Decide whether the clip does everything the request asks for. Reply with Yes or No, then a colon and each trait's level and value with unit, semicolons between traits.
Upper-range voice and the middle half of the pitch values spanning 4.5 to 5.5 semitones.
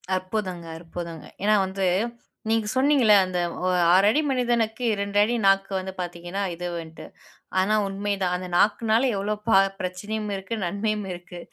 No: high, 195 Hz; average, 3.2 semitones